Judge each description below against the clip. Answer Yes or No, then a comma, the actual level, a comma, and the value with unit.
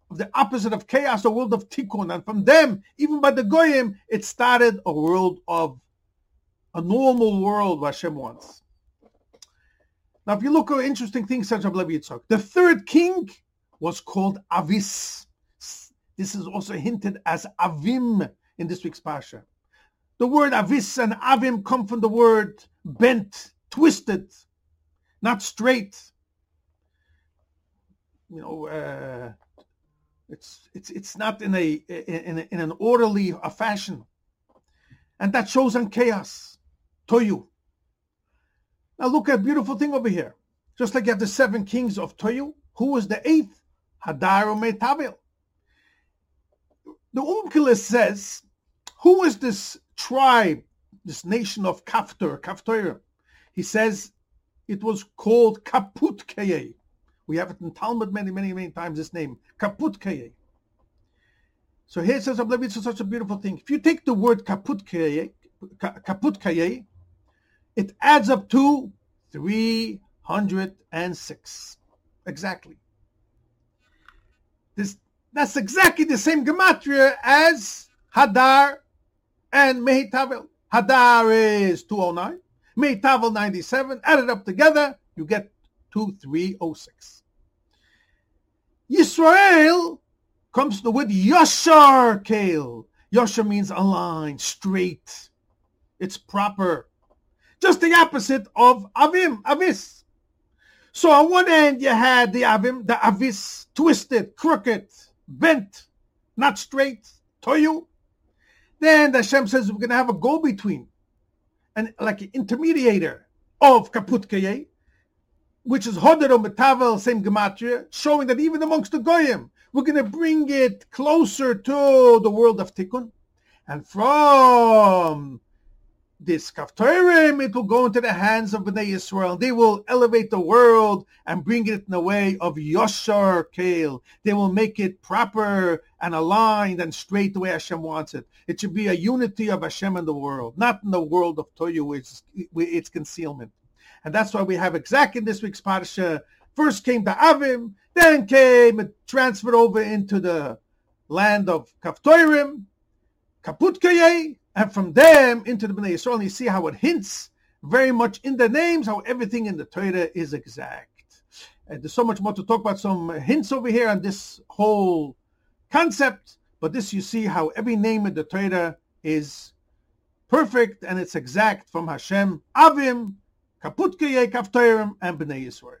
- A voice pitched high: Yes, high, 215 Hz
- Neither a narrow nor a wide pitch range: No, wide, 6.6 semitones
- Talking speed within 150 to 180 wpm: No, slow, 135 wpm